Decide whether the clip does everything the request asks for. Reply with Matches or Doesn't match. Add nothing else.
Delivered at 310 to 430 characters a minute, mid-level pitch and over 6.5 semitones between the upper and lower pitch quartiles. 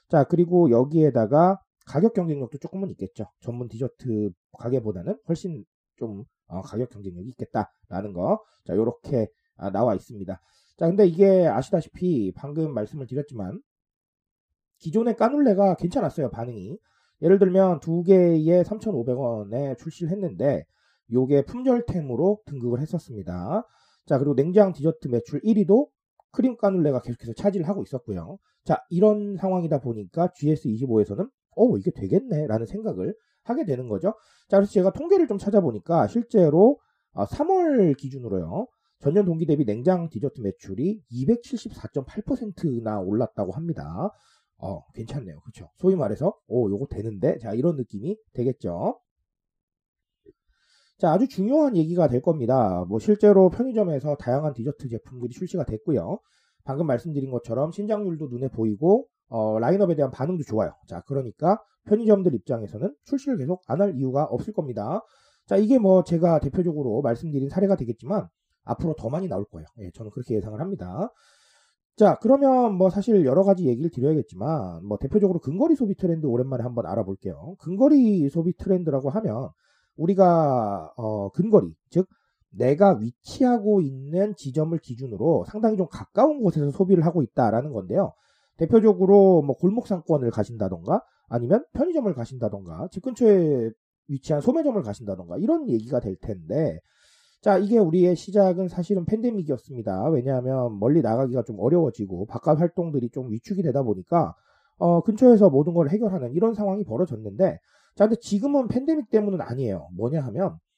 Matches